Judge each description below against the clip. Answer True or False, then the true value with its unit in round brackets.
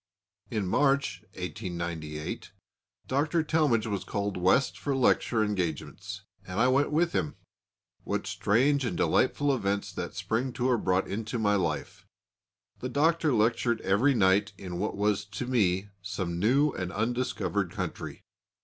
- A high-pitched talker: False (110 Hz)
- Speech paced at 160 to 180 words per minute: False (140 wpm)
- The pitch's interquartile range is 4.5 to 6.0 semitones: True (5.3 semitones)